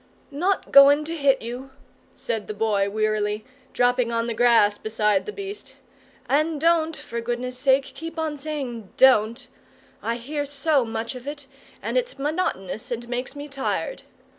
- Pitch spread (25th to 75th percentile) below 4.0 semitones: No, average, 4.5 semitones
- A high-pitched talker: Yes, very high, 255 Hz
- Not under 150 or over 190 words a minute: Yes, average, 160 wpm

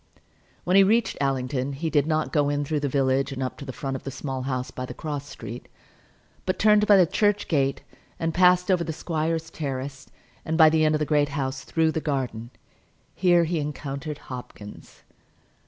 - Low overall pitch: No, medium, 145 Hz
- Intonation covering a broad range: No, average, 3.3 semitones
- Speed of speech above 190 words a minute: Yes, average, 200 wpm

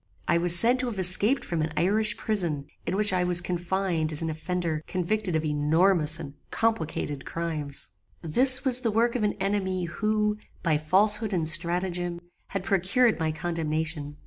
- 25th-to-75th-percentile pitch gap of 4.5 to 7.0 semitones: Yes, average, 4.8 semitones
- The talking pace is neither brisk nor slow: Yes, average, 170 wpm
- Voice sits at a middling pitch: Yes, medium, 180 Hz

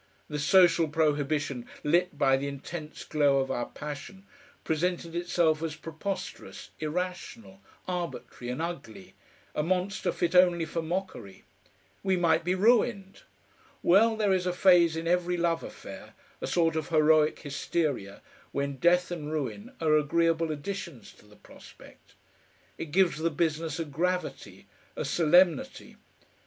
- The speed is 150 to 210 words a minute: No, average, 140 wpm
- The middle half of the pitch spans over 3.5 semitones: No, average, 3.2 semitones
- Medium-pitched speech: Yes, medium, 165 Hz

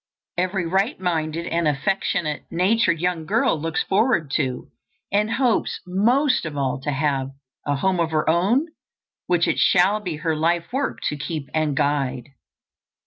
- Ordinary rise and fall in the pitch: Yes, average, 4.2 semitones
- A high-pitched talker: No, medium, 165 Hz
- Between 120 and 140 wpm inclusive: No, average, 155 wpm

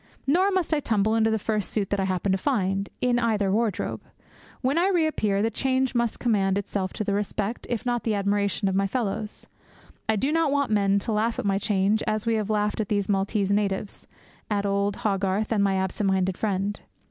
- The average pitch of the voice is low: No, high, 210 Hz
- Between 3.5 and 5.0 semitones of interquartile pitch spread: No, narrow, 2.6 semitones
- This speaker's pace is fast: Yes, fast, 215 wpm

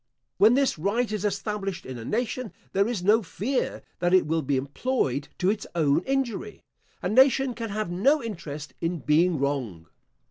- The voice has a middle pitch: No, high, 195 Hz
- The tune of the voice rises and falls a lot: Yes, wide, 7.0 semitones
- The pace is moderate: Yes, average, 175 wpm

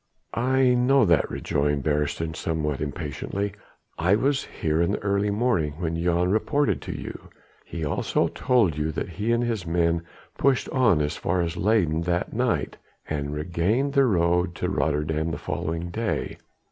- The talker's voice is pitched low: Yes, very low, 85 Hz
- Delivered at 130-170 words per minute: Yes, average, 160 wpm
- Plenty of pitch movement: Yes, wide, 5.9 semitones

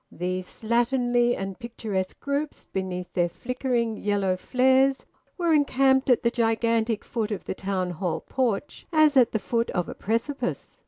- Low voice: No, high, 230 Hz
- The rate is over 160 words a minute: No, average, 155 wpm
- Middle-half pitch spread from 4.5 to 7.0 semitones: Yes, average, 5.1 semitones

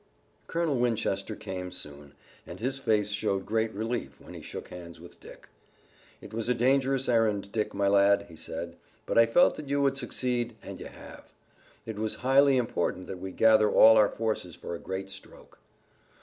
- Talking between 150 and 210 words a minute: Yes, average, 185 wpm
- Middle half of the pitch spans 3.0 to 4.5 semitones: Yes, average, 4.1 semitones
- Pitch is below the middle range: Yes, low, 110 Hz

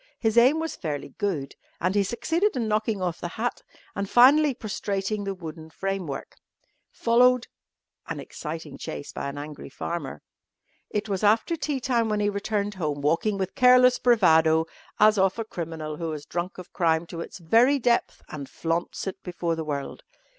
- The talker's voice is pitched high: Yes, high, 195 Hz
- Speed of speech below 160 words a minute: No, average, 175 wpm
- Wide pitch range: Yes, wide, 6.0 semitones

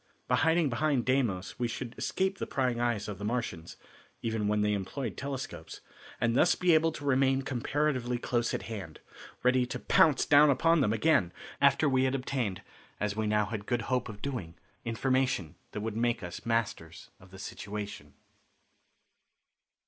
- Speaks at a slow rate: No, average, 170 wpm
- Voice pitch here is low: Yes, low, 120 Hz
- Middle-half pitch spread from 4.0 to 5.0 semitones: Yes, average, 4.5 semitones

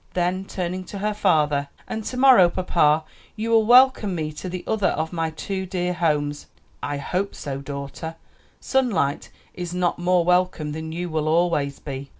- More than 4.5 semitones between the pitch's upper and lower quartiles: No, average, 3.7 semitones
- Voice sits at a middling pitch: Yes, medium, 175 Hz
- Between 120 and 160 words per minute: No, average, 170 wpm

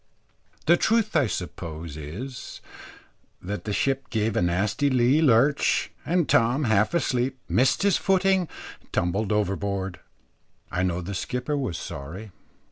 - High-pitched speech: No, low, 115 Hz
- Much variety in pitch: Yes, wide, 7.0 semitones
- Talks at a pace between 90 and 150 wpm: Yes, slow, 135 wpm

